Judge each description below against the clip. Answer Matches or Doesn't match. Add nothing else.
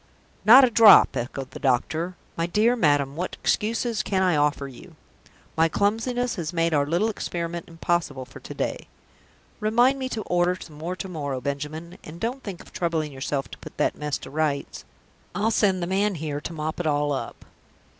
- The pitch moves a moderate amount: Doesn't match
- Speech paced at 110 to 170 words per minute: Doesn't match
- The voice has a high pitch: Doesn't match